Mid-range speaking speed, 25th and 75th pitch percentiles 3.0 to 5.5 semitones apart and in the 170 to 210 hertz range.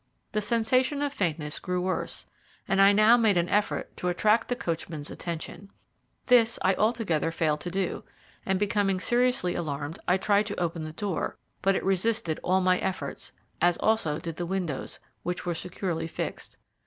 Yes: average, 170 wpm; average, 4.0 semitones; medium, 185 Hz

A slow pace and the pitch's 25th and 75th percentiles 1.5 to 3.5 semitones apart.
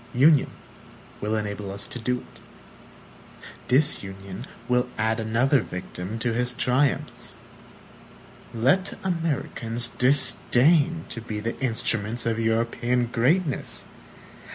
Yes: slow, 105 wpm; average, 3.1 semitones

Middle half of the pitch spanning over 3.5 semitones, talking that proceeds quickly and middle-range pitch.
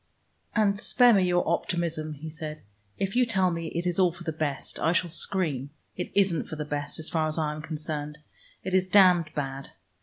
No: average, 3.2 semitones; fast, 210 wpm; medium, 165 Hz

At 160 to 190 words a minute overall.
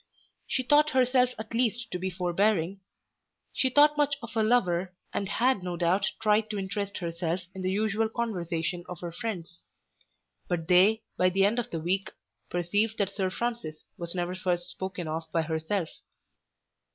Yes: average, 170 wpm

